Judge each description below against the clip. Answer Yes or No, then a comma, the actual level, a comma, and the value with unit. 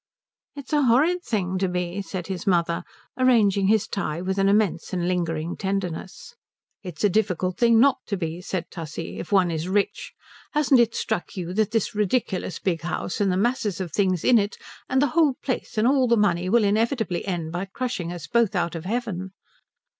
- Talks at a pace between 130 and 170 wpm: No, average, 195 wpm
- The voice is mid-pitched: No, high, 195 Hz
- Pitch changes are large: No, average, 4.5 semitones